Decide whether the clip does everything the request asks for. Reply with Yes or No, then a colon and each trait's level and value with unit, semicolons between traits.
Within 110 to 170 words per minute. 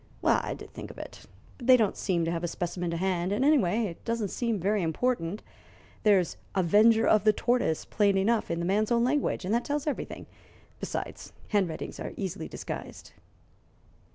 No: average, 180 wpm